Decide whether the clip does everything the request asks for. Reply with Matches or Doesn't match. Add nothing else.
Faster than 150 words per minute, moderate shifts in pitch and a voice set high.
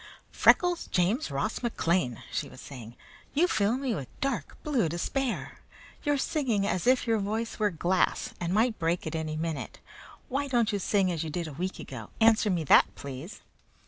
Doesn't match